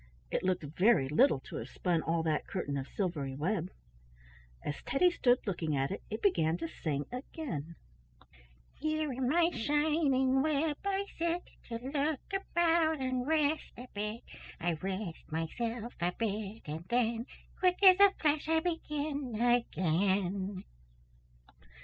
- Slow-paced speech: No, average, 145 wpm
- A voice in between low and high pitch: No, high, 235 Hz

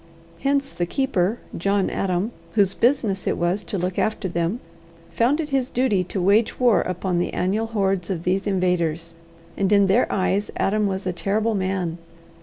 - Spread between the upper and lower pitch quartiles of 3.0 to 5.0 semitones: Yes, average, 3.3 semitones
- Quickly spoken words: No, average, 175 wpm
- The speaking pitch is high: Yes, high, 195 Hz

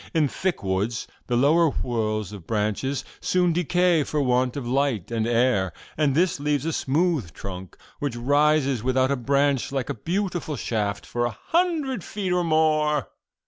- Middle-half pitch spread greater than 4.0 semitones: Yes, average, 5.2 semitones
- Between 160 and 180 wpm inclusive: Yes, average, 165 wpm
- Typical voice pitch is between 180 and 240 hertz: No, medium, 140 Hz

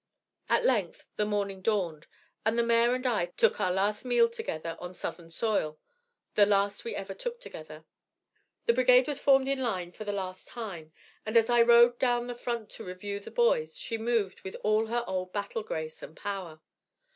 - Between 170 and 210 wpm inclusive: Yes, average, 190 wpm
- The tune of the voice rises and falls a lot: No, average, 4.4 semitones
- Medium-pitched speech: No, high, 215 Hz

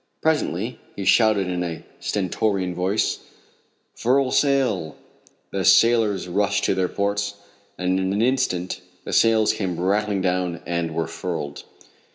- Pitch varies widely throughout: No, average, 3.4 semitones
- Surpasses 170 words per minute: No, slow, 135 wpm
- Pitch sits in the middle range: No, low, 100 Hz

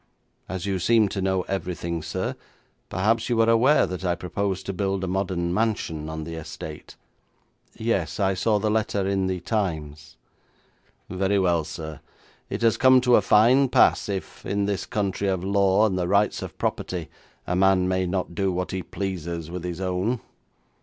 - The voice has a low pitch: Yes, very low, 95 Hz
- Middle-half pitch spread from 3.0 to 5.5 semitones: No, narrow, 2.5 semitones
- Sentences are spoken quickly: No, average, 180 wpm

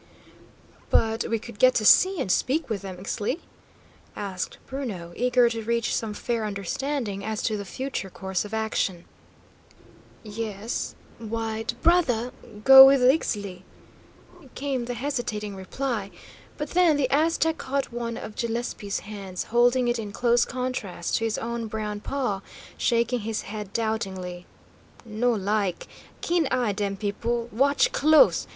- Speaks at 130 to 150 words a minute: Yes, average, 140 wpm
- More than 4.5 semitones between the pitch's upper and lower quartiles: No, average, 3.7 semitones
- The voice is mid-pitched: No, high, 230 Hz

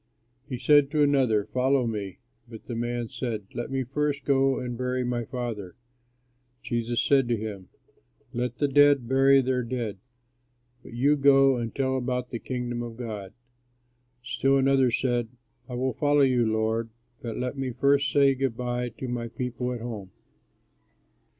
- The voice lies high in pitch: No, low, 125 Hz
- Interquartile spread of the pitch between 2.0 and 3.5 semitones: Yes, narrow, 2.4 semitones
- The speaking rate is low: No, average, 165 wpm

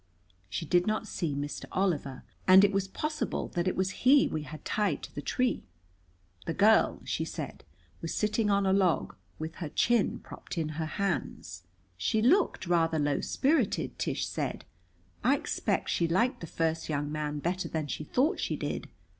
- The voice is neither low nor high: Yes, medium, 175 Hz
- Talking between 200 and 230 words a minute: No, average, 180 wpm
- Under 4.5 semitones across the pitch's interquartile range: No, average, 5.3 semitones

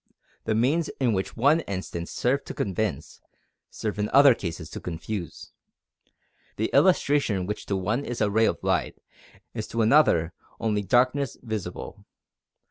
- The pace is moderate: Yes, average, 145 wpm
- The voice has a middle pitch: No, low, 110 Hz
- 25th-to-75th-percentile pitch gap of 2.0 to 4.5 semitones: No, average, 5.3 semitones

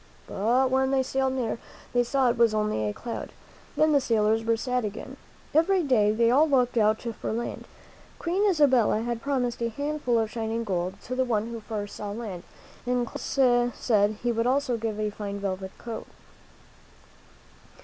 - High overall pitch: Yes, high, 235 Hz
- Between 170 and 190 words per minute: Yes, average, 180 wpm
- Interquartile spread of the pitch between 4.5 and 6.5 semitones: No, average, 3.3 semitones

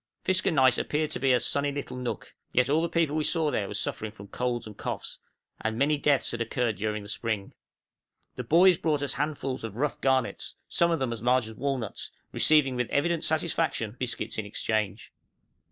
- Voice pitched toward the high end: No, low, 130 Hz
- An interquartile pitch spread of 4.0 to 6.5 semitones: Yes, average, 4.9 semitones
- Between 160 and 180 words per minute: No, average, 195 wpm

